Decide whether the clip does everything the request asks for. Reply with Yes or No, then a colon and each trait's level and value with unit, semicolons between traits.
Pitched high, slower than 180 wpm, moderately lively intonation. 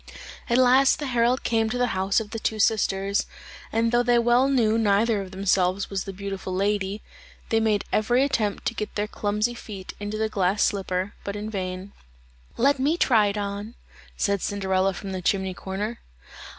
No: high, 210 Hz; average, 185 wpm; average, 3.0 semitones